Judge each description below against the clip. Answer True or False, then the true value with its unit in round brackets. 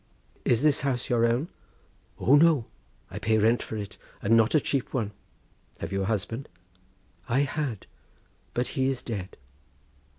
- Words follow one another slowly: False (160 wpm)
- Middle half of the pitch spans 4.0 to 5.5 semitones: False (3.6 semitones)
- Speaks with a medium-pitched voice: False (120 Hz)